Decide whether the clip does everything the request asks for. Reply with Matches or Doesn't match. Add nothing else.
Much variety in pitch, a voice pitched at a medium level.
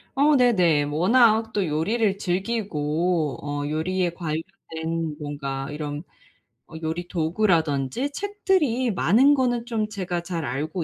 Matches